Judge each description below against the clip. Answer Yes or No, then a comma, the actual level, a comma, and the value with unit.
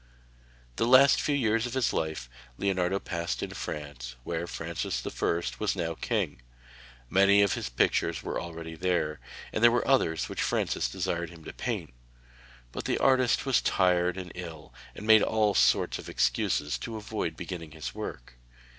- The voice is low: Yes, very low, 90 Hz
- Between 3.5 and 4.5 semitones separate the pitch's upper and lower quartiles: No, average, 4.9 semitones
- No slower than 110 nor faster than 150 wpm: No, average, 165 wpm